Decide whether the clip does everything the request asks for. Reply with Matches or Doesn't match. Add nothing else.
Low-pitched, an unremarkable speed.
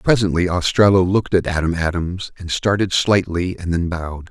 Matches